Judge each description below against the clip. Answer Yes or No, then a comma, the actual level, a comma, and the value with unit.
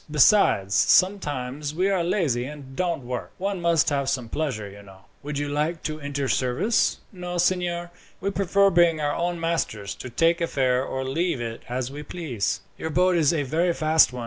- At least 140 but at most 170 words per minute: No, average, 195 wpm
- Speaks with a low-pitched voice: No, medium, 150 Hz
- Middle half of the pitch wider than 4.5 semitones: Yes, average, 4.9 semitones